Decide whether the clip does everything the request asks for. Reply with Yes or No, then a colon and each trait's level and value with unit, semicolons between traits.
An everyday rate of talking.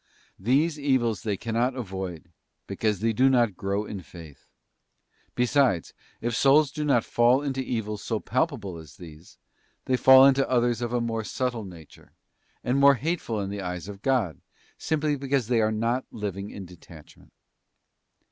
Yes: average, 160 wpm